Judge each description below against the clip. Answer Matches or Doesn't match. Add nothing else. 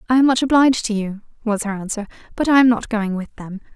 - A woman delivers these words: Matches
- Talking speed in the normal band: Doesn't match